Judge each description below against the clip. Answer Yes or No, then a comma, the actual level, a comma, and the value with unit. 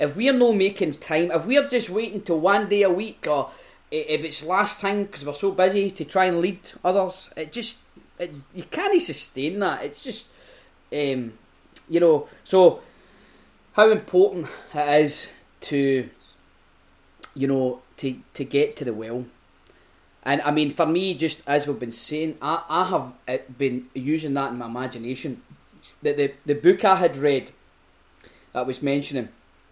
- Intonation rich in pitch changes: Yes, wide, 6.0 semitones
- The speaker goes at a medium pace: Yes, average, 170 wpm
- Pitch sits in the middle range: Yes, medium, 155 Hz